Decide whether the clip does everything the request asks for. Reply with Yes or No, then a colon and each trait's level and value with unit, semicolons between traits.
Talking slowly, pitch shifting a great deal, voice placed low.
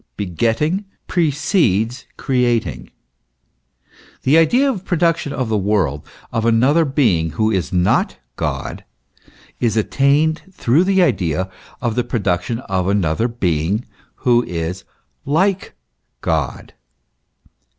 Yes: slow, 110 wpm; wide, 7.9 semitones; low, 120 Hz